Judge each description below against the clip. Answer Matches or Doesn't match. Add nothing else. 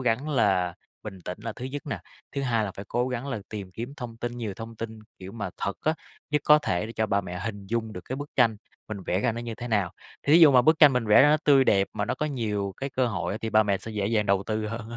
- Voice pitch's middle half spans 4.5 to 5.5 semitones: Doesn't match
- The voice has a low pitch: Matches